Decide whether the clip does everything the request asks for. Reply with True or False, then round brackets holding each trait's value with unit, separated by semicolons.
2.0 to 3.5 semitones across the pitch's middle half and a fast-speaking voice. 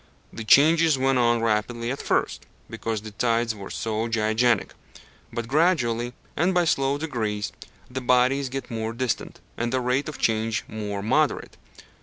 False (3.2 semitones; 155 wpm)